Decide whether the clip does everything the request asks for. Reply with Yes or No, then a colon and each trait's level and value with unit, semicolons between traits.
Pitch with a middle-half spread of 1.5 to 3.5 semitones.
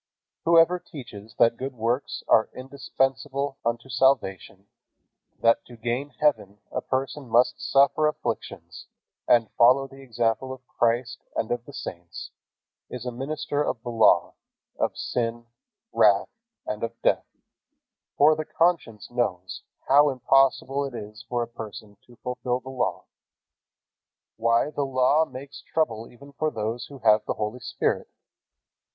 Yes: average, 3.1 semitones